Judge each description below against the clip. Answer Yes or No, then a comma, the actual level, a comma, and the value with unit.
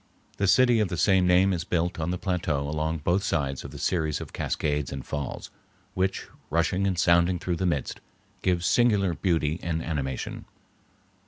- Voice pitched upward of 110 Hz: No, very low, 85 Hz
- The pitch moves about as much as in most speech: Yes, average, 3.0 semitones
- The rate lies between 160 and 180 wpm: Yes, average, 175 wpm